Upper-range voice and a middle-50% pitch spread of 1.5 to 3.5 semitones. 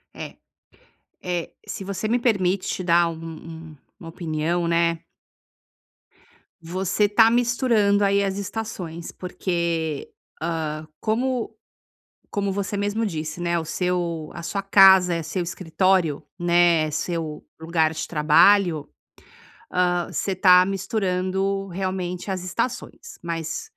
No: medium, 180 Hz; average, 3.1 semitones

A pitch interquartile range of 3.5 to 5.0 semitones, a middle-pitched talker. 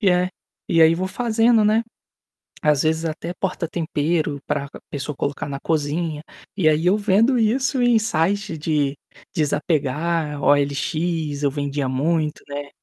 Yes: average, 4.4 semitones; medium, 160 Hz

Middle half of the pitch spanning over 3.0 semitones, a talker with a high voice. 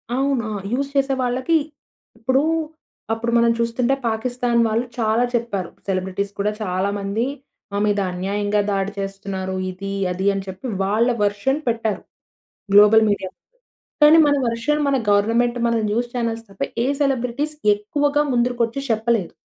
Yes: average, 3.5 semitones; high, 225 Hz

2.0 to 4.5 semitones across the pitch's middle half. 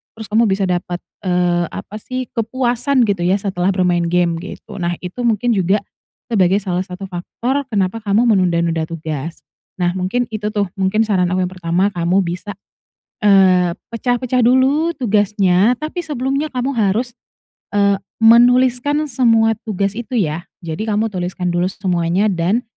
No: average, 4.9 semitones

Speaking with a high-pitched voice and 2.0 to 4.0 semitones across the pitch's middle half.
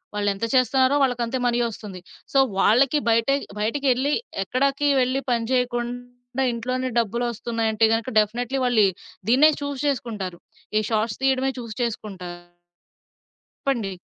Yes: high, 240 Hz; average, 2.7 semitones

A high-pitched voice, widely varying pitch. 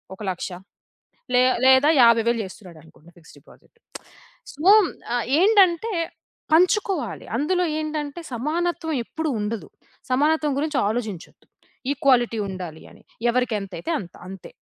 Yes: very high, 260 Hz; wide, 7.3 semitones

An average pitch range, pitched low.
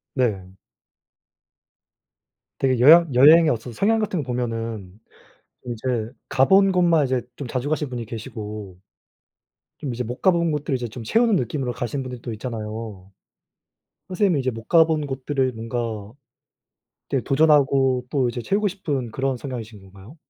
Yes: average, 4.7 semitones; low, 130 Hz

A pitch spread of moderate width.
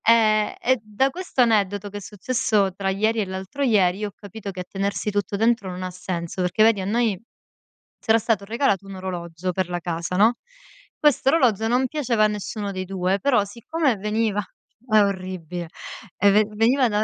Yes: average, 3.4 semitones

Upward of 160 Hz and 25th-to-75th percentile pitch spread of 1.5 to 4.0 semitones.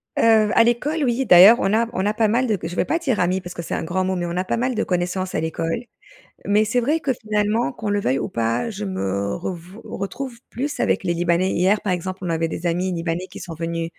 No: high, 190 Hz; average, 4.8 semitones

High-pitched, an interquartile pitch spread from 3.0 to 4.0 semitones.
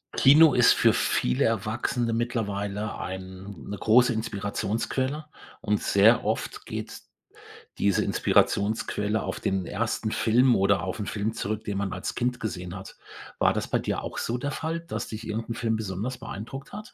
No: low, 110 Hz; average, 3.3 semitones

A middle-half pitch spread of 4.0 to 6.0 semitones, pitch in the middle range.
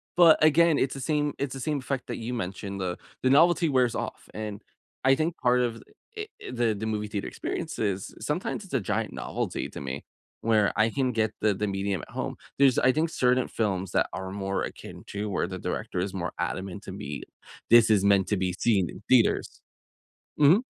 No: wide, 5.4 semitones; low, 110 Hz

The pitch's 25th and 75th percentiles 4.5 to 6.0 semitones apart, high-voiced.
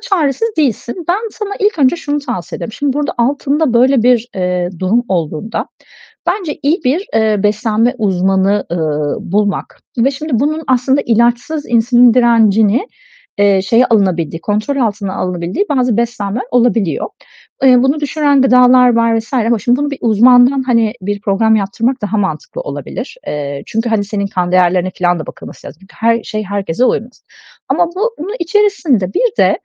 Yes: average, 5.3 semitones; high, 235 Hz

